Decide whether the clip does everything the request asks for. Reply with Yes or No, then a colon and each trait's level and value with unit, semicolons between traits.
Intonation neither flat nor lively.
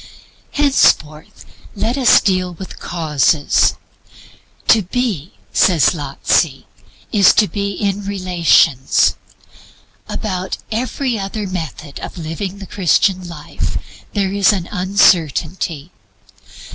Yes: average, 3.7 semitones